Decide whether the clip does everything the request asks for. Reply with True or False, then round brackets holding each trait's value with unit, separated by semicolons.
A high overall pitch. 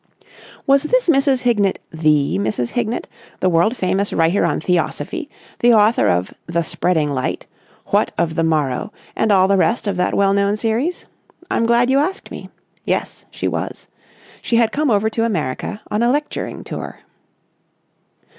True (205 Hz)